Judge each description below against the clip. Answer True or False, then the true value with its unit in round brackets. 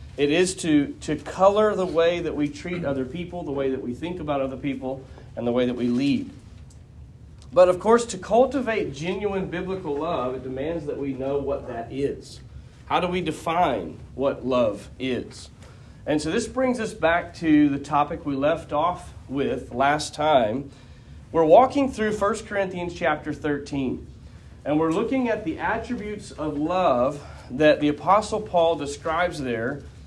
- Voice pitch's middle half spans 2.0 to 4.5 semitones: False (4.9 semitones)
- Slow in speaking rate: False (170 wpm)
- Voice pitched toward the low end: False (155 Hz)